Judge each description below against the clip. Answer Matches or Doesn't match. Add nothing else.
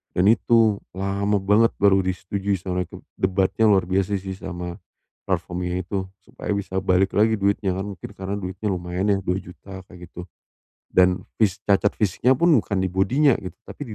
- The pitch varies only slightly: Matches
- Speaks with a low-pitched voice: Matches